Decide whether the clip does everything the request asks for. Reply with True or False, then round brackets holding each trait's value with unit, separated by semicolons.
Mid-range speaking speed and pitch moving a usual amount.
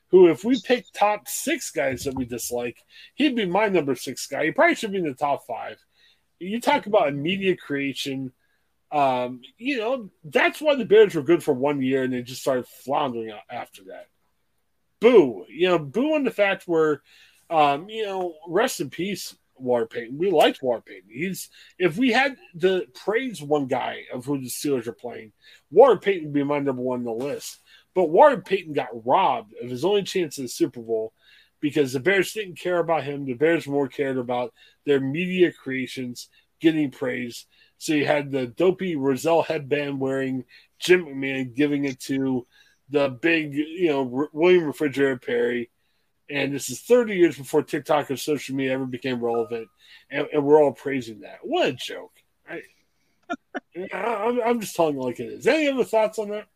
False (190 wpm; 5.9 semitones)